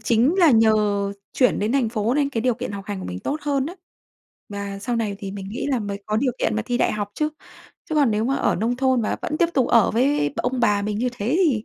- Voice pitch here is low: No, high, 230 Hz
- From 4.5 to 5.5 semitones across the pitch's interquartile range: No, average, 4.0 semitones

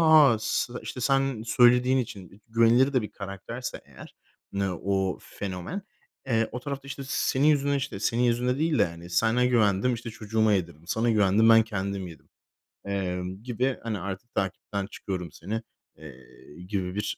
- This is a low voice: Yes, low, 110 Hz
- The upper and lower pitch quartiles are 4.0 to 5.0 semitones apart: Yes, average, 4.5 semitones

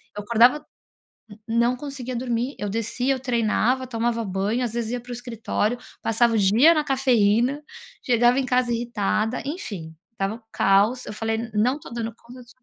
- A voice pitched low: No, high, 235 Hz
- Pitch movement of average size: No, narrow, 2.2 semitones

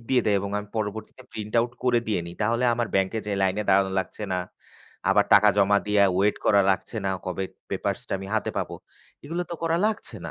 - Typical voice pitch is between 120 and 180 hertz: No, low, 105 Hz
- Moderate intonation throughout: Yes, average, 3.2 semitones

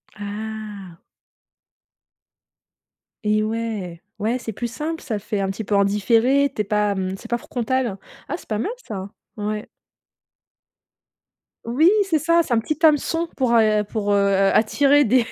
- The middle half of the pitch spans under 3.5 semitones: No, average, 3.8 semitones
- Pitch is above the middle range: Yes, high, 220 Hz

